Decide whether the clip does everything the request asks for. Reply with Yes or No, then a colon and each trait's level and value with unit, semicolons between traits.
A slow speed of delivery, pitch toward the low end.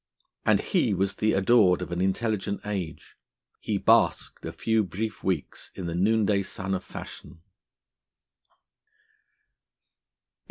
Yes: slow, 120 wpm; very low, 95 Hz